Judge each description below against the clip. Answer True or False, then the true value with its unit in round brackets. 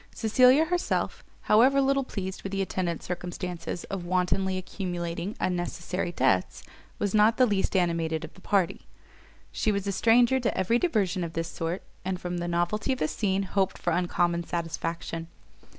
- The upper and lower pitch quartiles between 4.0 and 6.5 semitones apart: False (3.4 semitones)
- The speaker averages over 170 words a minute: False (165 wpm)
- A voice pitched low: False (185 Hz)